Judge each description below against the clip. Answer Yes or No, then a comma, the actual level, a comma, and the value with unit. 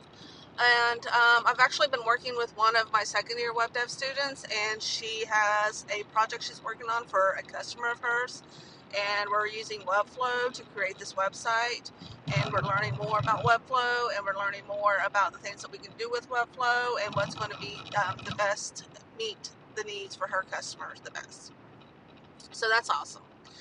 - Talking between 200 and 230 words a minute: No, average, 190 wpm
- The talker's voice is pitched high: Yes, high, 225 Hz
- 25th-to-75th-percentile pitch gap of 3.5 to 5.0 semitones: No, average, 3.0 semitones